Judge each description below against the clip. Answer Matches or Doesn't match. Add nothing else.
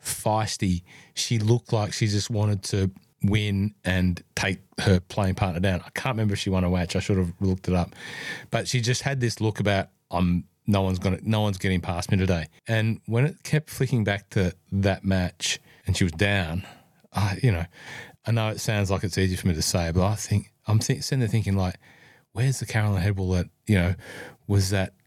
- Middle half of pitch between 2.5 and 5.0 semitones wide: Matches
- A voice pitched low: Matches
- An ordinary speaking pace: Doesn't match